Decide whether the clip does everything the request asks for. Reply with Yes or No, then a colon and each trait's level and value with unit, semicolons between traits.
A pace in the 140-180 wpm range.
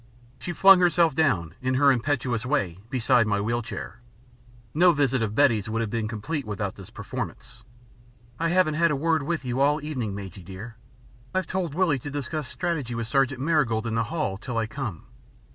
No: average, 195 wpm